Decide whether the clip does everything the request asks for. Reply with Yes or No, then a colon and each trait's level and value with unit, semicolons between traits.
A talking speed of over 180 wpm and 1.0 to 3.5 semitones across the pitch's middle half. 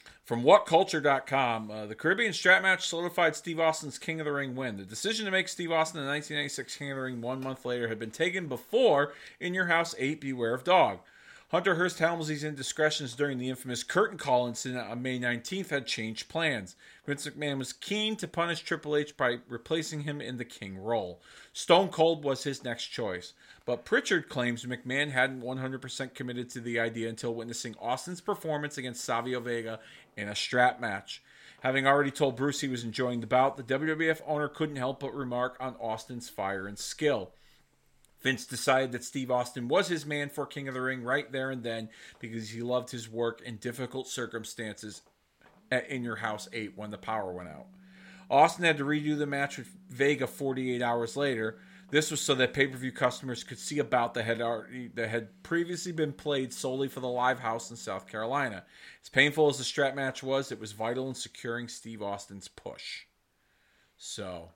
No: average, 190 wpm; average, 4.2 semitones